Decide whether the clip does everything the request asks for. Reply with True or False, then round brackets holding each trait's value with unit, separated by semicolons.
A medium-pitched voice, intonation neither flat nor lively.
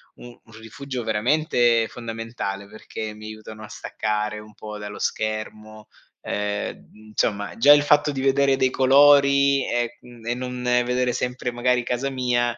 False (120 Hz; 3.1 semitones)